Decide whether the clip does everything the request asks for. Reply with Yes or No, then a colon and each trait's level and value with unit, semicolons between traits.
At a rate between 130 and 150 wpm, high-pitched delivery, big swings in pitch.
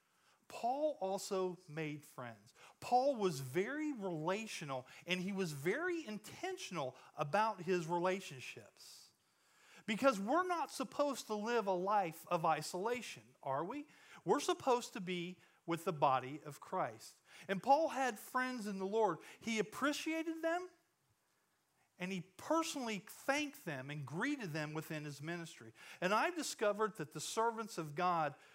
Yes: average, 140 wpm; high, 195 Hz; wide, 8.0 semitones